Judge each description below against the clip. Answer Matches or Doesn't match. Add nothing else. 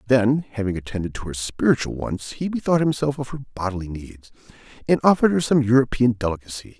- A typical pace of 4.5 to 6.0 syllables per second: Doesn't match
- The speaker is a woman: Doesn't match